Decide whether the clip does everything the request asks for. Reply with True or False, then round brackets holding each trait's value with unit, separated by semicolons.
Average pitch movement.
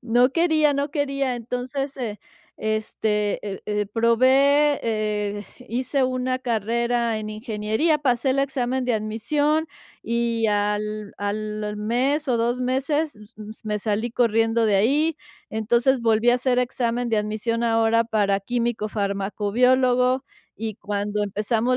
True (3.3 semitones)